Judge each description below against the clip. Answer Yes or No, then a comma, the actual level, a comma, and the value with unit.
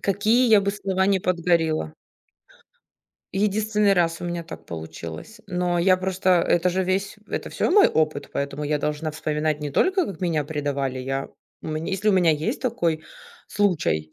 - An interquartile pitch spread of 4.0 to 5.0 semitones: Yes, average, 4.6 semitones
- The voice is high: No, medium, 175 Hz